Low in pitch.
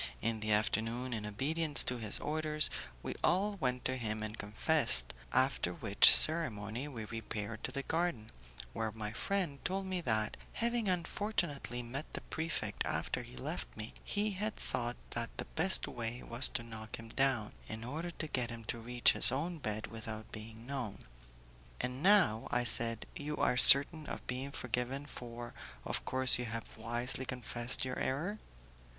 Yes: low, 125 Hz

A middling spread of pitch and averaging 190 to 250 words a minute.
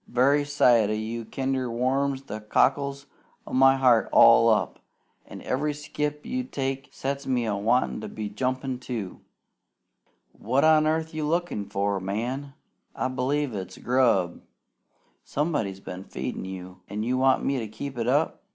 No: average, 4.3 semitones; average, 160 wpm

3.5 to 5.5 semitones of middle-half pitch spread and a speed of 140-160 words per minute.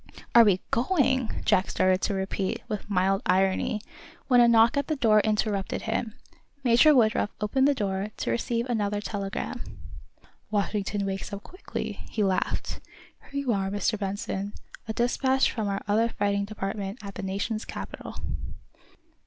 No: average, 3.0 semitones; average, 155 wpm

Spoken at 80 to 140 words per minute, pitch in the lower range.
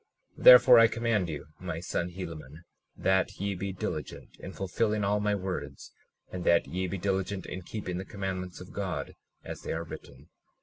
No: average, 180 wpm; very low, 95 Hz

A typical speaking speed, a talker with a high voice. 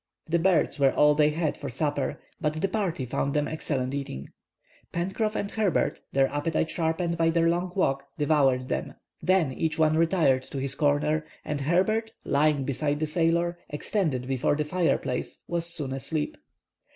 No: average, 165 wpm; medium, 155 Hz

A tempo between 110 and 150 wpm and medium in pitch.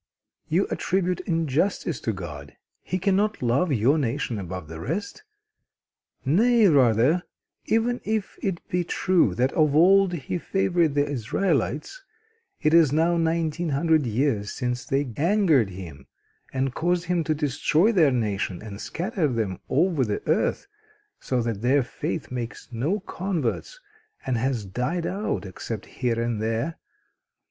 Yes: average, 140 wpm; medium, 145 Hz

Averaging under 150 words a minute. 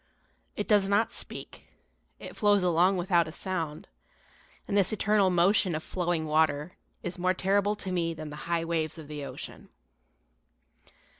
No: average, 155 wpm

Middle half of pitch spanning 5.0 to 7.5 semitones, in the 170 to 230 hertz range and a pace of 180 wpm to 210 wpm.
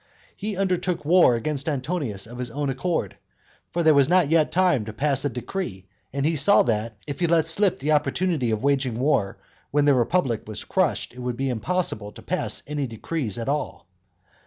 No: wide, 5.5 semitones; medium, 140 Hz; average, 195 wpm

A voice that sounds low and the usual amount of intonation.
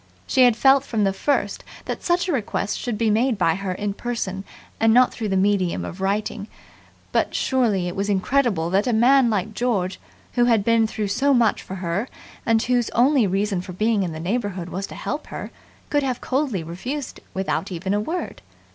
No: high, 215 Hz; average, 4.3 semitones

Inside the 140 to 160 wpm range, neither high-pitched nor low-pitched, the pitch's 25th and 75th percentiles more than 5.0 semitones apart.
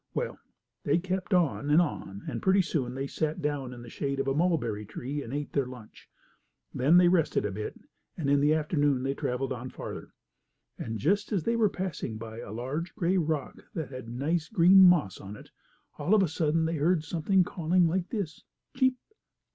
No: average, 200 wpm; medium, 150 Hz; wide, 5.5 semitones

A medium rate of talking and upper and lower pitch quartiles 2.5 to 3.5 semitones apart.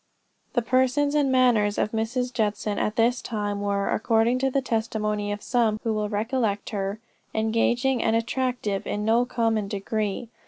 Yes: average, 160 wpm; average, 2.9 semitones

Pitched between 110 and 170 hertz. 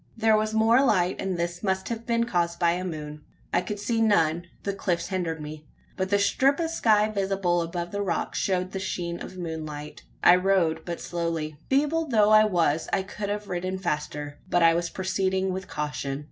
No: medium, 185 Hz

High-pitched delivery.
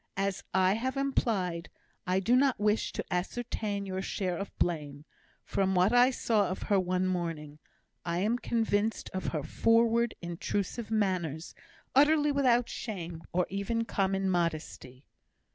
Yes: high, 195 Hz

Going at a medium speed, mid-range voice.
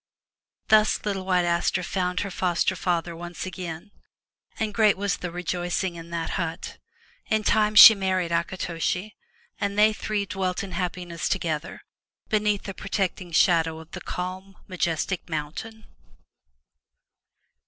No: slow, 130 wpm; medium, 180 Hz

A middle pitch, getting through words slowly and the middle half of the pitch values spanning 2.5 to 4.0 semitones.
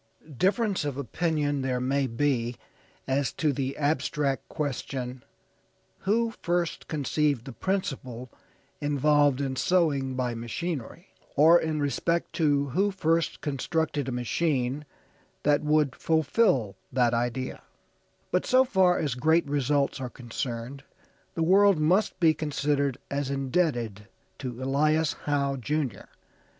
Yes: medium, 145 Hz; slow, 120 wpm; average, 3.6 semitones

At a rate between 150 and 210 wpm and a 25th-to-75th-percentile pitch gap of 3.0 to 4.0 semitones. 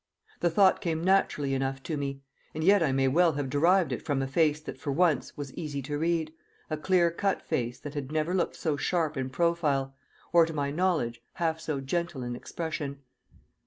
Yes: average, 200 wpm; average, 3.7 semitones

